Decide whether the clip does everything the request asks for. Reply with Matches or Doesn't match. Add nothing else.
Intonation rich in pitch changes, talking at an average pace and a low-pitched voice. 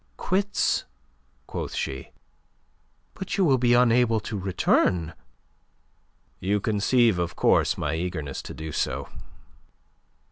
Doesn't match